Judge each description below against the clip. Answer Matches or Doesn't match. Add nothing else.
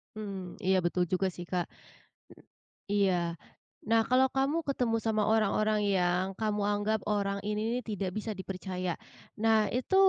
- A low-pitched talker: Doesn't match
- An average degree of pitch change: Matches